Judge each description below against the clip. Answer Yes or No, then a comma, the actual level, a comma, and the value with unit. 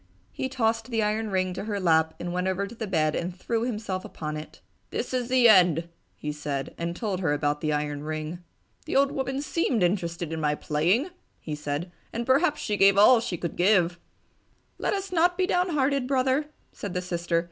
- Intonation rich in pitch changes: Yes, wide, 7.0 semitones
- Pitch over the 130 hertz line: Yes, high, 190 Hz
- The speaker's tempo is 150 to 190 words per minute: No, average, 200 wpm